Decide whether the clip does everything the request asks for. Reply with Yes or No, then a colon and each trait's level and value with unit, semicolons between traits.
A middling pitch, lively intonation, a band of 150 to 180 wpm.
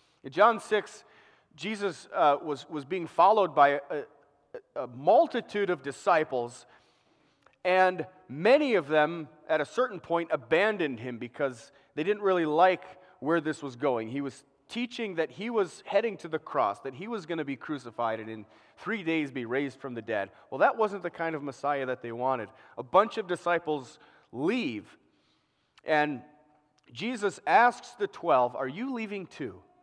Yes: medium, 160 Hz; wide, 6.1 semitones; average, 170 wpm